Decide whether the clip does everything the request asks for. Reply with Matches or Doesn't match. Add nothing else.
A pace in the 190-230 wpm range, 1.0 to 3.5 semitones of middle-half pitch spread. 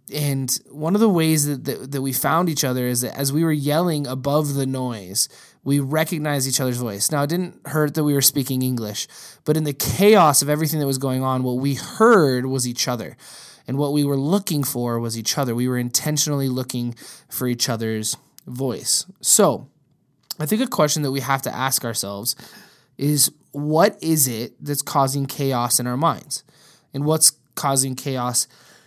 Matches